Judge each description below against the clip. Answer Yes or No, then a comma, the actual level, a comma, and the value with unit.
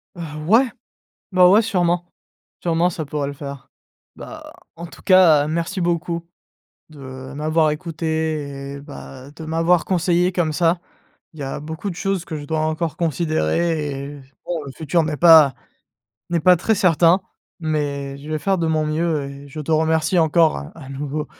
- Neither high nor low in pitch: Yes, medium, 160 Hz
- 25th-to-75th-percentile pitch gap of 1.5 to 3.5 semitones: Yes, average, 2.8 semitones